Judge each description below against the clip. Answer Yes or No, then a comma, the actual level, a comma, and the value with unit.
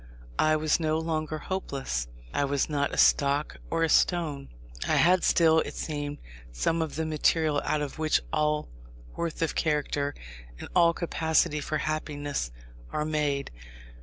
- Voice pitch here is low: No, medium, 155 Hz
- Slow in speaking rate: No, average, 155 wpm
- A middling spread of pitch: No, narrow, 1.8 semitones